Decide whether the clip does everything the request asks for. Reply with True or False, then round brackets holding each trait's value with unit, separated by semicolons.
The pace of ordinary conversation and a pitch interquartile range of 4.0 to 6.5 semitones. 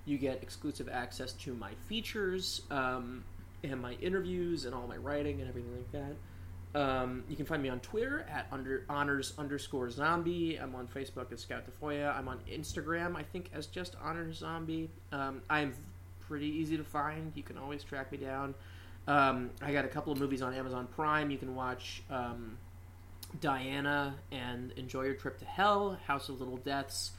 True (185 wpm; 4.5 semitones)